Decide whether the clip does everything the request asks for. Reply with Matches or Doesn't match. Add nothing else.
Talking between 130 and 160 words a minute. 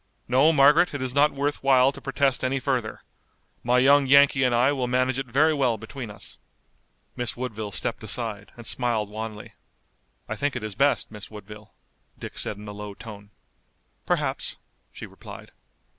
Doesn't match